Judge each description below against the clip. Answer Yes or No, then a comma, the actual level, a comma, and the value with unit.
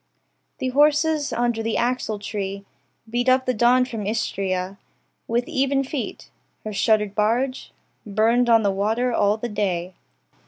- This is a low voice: No, high, 225 Hz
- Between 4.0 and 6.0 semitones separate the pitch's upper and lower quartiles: No, average, 3.6 semitones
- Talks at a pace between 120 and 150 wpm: Yes, average, 140 wpm